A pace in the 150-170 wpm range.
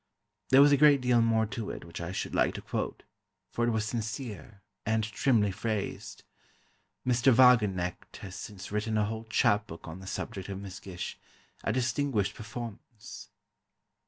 Yes: average, 160 wpm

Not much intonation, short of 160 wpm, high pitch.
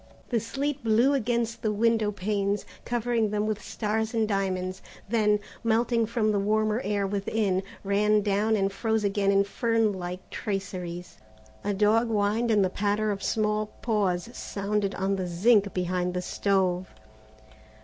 Yes: narrow, 2.2 semitones; average, 150 wpm; high, 210 Hz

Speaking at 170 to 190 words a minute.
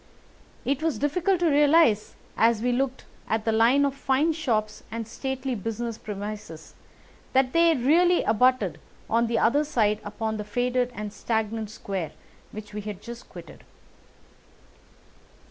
No: average, 145 wpm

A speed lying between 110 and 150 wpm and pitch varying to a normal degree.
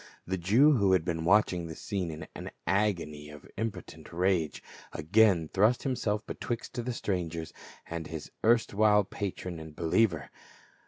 Yes: average, 145 wpm; average, 4.7 semitones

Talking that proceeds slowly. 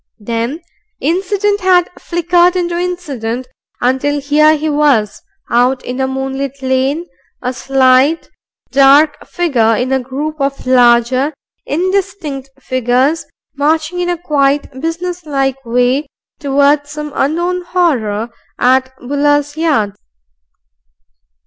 Yes: slow, 110 wpm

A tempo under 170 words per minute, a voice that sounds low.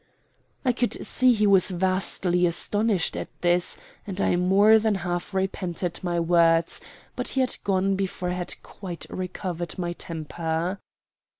No: average, 145 wpm; medium, 185 Hz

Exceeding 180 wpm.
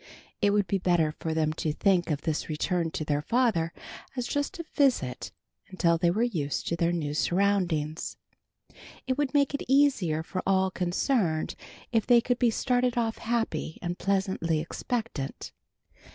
No: average, 165 wpm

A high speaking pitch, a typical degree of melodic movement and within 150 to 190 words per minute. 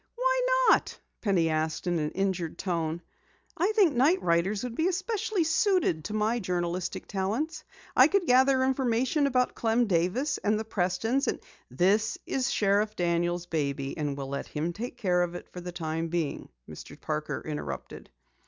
No: high, 200 Hz; wide, 7.3 semitones; average, 165 wpm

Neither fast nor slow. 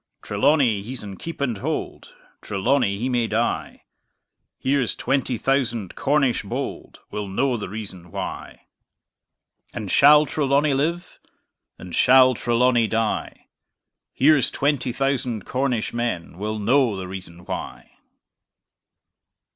No: slow, 115 wpm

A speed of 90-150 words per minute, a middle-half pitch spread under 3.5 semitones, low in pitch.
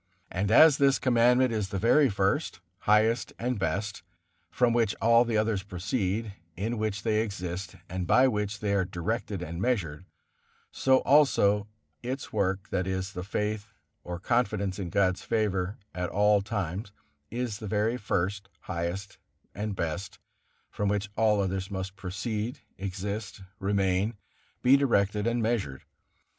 Yes: average, 145 wpm; average, 3.1 semitones; low, 105 Hz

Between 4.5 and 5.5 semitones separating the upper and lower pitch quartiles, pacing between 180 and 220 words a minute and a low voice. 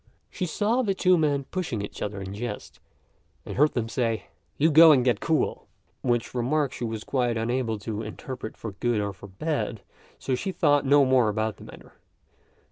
Yes: average, 5.2 semitones; average, 185 wpm; low, 125 Hz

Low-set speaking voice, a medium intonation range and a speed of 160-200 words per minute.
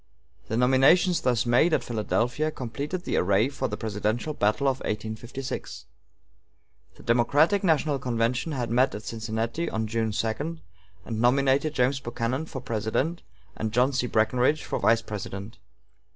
No: low, 125 Hz; average, 3.9 semitones; average, 145 wpm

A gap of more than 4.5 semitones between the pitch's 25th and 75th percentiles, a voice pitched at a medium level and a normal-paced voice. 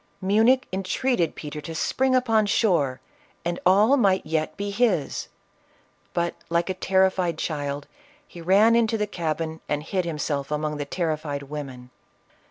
Yes: average, 5.2 semitones; medium, 170 Hz; average, 145 wpm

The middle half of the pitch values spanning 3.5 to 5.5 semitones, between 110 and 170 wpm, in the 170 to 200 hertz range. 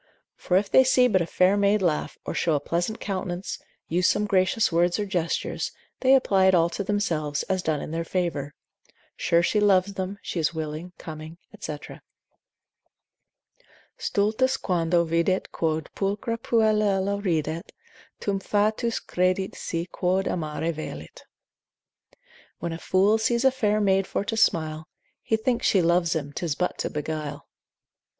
Yes: average, 3.8 semitones; average, 155 wpm; medium, 185 Hz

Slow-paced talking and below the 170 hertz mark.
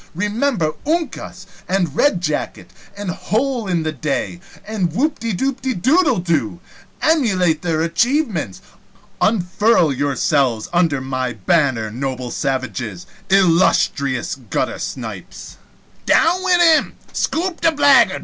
No: slow, 100 wpm; medium, 180 Hz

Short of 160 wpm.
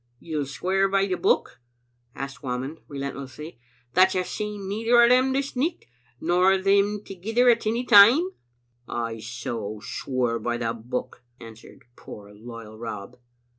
Yes: average, 150 wpm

